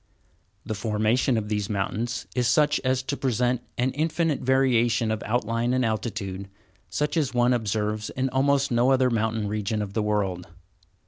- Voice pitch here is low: Yes, low, 120 Hz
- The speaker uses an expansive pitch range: No, average, 3.4 semitones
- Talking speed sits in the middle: Yes, average, 165 wpm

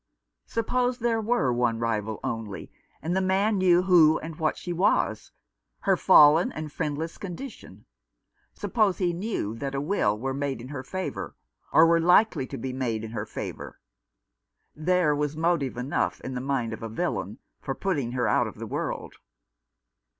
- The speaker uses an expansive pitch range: Yes, wide, 7.0 semitones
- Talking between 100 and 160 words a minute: No, average, 170 wpm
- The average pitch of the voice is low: No, medium, 150 Hz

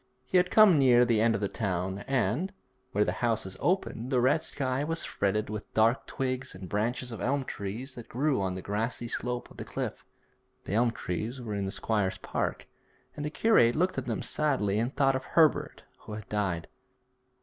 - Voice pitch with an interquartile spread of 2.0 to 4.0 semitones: No, average, 4.5 semitones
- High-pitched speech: No, low, 120 Hz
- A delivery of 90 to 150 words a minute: No, average, 200 wpm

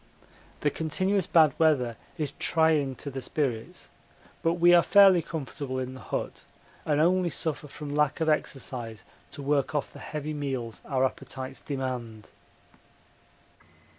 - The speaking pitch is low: No, medium, 145 Hz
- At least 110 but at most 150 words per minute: Yes, average, 140 wpm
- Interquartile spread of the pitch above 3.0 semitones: Yes, average, 3.5 semitones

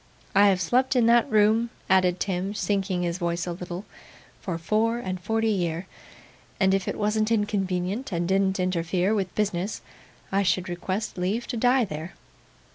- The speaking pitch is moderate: No, high, 195 Hz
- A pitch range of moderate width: Yes, average, 3.2 semitones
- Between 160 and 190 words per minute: Yes, average, 165 wpm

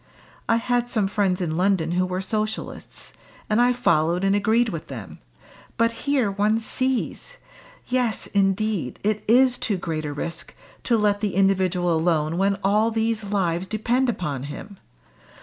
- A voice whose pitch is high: Yes, high, 200 Hz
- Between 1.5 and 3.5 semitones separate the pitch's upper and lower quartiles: No, average, 4.2 semitones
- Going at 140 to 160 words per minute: Yes, average, 155 wpm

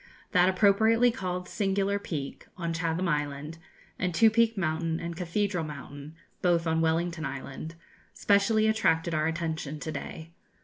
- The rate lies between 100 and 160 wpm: Yes, average, 140 wpm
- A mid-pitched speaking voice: Yes, medium, 170 Hz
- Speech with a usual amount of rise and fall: Yes, average, 3.7 semitones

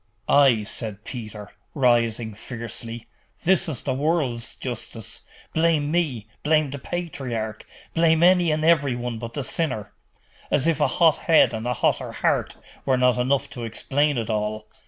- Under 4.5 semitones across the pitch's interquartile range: No, average, 5.2 semitones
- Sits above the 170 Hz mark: No, low, 130 Hz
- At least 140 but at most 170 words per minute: Yes, average, 155 wpm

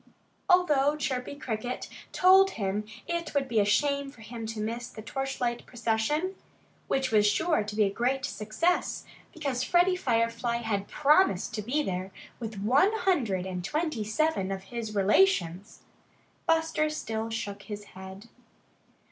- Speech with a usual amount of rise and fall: No, wide, 6.2 semitones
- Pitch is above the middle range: Yes, high, 235 Hz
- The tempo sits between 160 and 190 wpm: No, average, 150 wpm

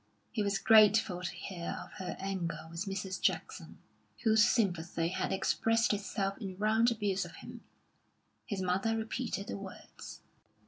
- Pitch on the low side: No, high, 195 Hz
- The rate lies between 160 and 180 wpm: No, average, 145 wpm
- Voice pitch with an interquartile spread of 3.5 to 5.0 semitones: No, average, 2.9 semitones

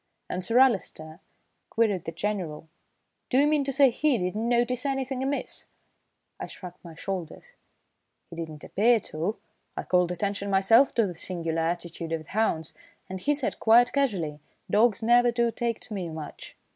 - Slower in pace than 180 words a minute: Yes, average, 170 wpm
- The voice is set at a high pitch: Yes, high, 205 Hz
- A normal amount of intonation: No, wide, 6.1 semitones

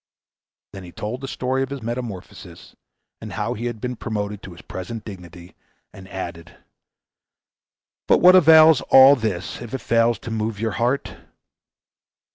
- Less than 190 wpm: Yes, average, 155 wpm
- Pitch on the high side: No, low, 115 Hz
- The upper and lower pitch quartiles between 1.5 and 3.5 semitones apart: No, average, 4.8 semitones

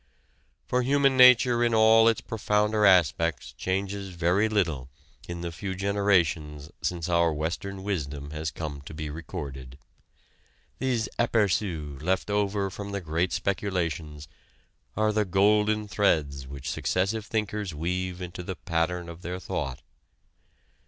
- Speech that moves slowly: Yes, slow, 130 wpm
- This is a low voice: Yes, very low, 90 Hz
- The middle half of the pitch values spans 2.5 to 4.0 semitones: No, average, 4.6 semitones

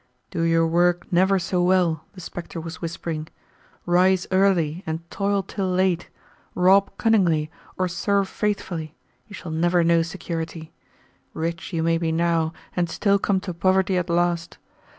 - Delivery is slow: No, average, 150 wpm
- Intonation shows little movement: Yes, narrow, 2.3 semitones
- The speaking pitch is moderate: Yes, medium, 175 Hz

